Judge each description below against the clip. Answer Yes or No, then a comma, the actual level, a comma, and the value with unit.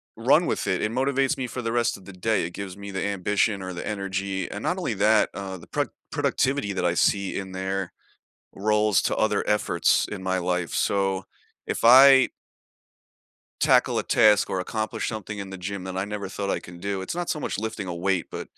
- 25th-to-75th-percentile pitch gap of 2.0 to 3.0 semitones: Yes, narrow, 2.4 semitones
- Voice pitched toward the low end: Yes, low, 100 Hz